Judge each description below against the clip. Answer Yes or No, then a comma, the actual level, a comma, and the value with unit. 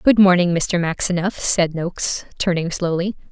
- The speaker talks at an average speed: Yes, average, 145 wpm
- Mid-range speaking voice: Yes, medium, 175 Hz